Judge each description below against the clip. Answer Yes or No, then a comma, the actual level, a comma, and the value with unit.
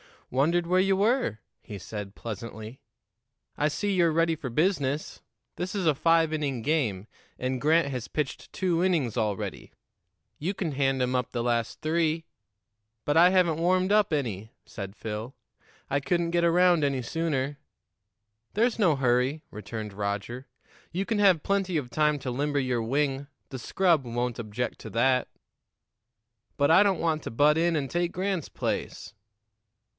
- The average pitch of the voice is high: No, medium, 145 Hz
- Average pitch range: No, wide, 5.8 semitones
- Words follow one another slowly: No, average, 160 wpm